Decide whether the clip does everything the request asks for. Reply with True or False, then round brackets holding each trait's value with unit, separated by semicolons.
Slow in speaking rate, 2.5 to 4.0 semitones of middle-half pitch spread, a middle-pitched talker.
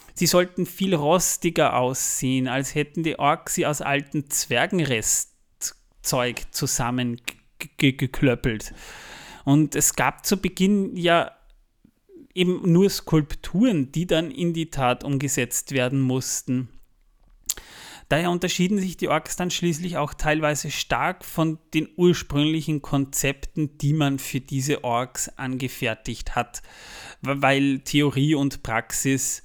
False (120 wpm; 4.5 semitones; 145 Hz)